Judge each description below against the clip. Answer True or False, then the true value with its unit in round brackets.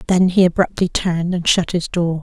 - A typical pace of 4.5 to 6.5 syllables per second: True (5.4 syllables/s)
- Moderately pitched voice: True (175 Hz)